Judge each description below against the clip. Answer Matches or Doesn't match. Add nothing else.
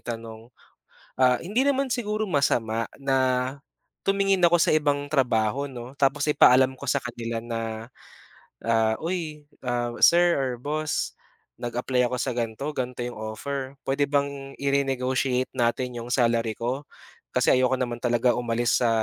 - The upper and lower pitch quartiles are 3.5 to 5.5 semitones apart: Doesn't match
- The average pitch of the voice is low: Matches